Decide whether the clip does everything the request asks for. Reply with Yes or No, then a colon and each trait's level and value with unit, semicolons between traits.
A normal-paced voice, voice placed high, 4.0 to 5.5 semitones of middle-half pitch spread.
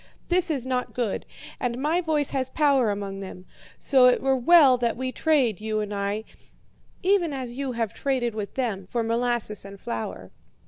Yes: average, 180 wpm; high, 245 Hz; average, 4.4 semitones